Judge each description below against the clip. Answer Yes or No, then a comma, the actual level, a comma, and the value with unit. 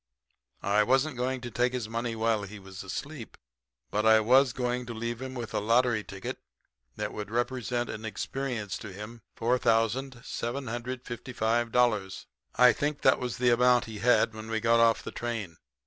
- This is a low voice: Yes, low, 120 Hz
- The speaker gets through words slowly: No, average, 165 wpm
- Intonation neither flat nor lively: No, narrow, 2.2 semitones